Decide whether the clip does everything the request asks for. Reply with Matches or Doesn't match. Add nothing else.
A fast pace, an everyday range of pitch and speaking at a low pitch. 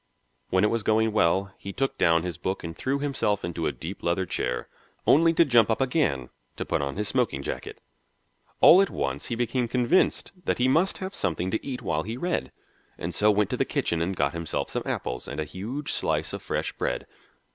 Doesn't match